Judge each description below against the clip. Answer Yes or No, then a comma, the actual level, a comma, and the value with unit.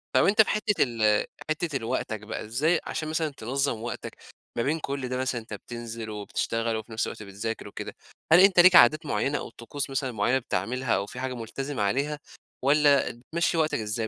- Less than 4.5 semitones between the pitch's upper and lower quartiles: No, average, 4.8 semitones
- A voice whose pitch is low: Yes, low, 125 Hz